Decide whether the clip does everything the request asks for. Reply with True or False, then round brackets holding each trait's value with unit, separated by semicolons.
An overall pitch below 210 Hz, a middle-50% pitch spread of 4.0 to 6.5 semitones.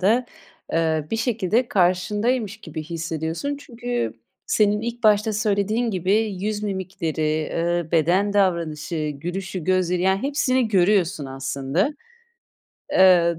True (190 Hz; 4.5 semitones)